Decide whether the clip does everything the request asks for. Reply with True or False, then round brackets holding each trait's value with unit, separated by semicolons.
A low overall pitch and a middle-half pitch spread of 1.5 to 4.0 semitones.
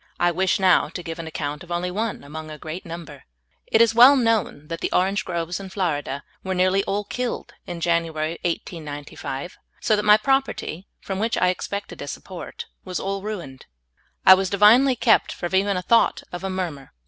False (185 Hz; 3.6 semitones)